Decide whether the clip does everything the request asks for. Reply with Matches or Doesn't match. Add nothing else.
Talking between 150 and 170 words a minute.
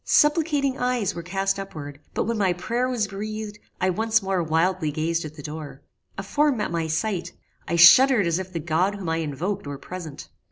Doesn't match